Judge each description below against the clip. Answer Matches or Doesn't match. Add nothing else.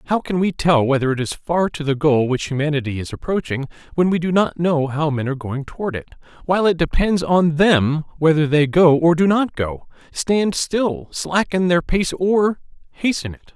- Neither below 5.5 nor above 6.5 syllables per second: Doesn't match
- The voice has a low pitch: Doesn't match